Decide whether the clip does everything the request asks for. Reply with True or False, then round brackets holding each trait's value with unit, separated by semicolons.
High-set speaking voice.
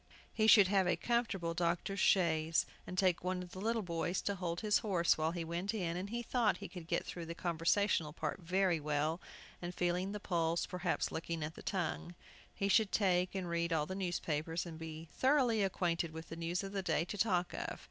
False (175 Hz)